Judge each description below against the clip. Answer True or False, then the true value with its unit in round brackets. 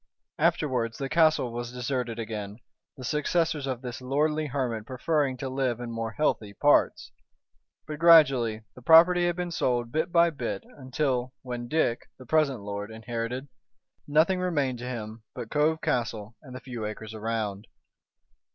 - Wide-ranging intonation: False (4.6 semitones)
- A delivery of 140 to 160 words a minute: True (155 wpm)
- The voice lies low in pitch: True (125 Hz)